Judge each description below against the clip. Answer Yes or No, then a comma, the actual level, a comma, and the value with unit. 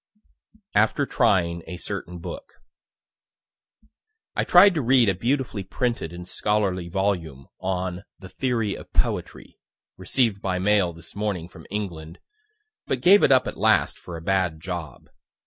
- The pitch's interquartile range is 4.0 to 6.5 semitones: Yes, average, 4.7 semitones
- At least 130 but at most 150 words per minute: Yes, average, 145 wpm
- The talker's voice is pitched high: No, very low, 95 Hz